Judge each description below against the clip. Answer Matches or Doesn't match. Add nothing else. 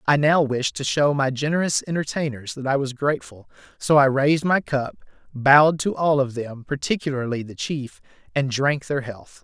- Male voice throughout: Matches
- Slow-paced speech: Doesn't match